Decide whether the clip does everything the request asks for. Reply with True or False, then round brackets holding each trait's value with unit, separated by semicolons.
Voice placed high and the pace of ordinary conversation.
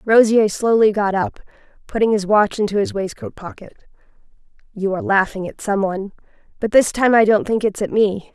True (210 Hz; 180 wpm)